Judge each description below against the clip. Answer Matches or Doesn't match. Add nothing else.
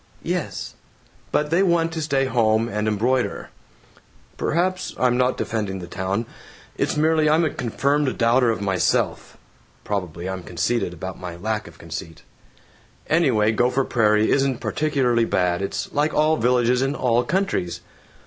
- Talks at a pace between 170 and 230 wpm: Doesn't match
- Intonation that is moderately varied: Doesn't match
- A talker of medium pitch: Doesn't match